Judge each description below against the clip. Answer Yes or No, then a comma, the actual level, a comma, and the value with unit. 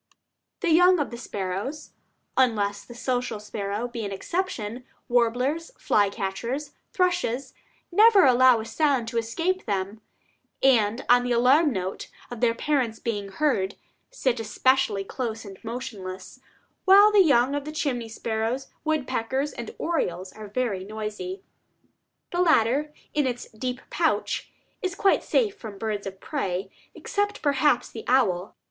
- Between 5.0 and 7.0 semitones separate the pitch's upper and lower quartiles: Yes, wide, 5.5 semitones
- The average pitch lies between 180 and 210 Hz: No, high, 245 Hz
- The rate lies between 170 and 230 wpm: No, average, 140 wpm